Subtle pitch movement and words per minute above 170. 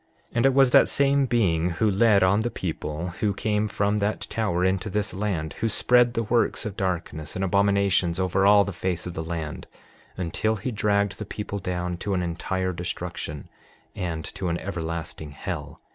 No: average, 3.3 semitones; average, 185 wpm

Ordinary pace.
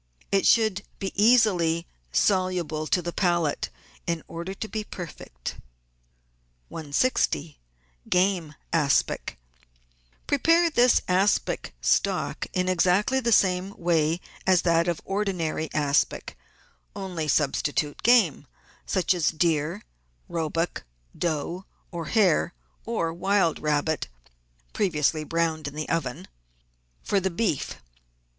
No: slow, 110 wpm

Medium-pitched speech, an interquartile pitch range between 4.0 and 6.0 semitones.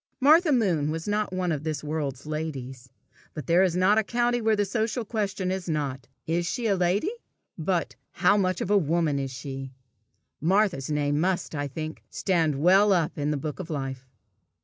Yes: medium, 170 Hz; average, 5.2 semitones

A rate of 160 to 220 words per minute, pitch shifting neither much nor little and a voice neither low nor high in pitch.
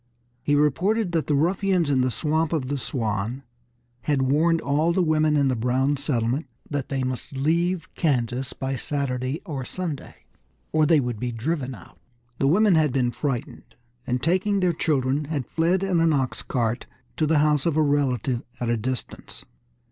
Yes: average, 180 wpm; average, 4.0 semitones; medium, 145 Hz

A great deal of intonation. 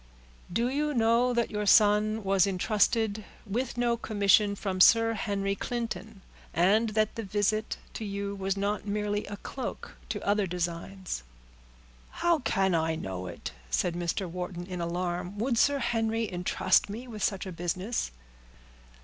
No: average, 3.2 semitones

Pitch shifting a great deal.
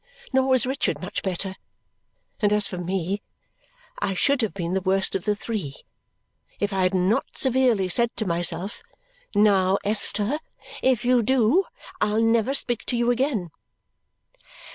No: average, 4.3 semitones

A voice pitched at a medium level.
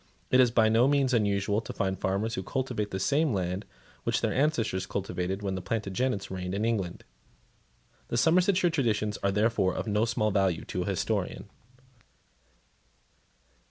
No: low, 105 Hz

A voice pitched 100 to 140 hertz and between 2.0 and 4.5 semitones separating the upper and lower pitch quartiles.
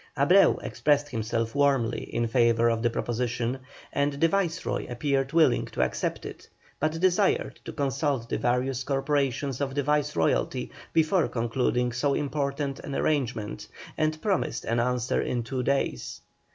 Yes: low, 135 Hz; average, 3.5 semitones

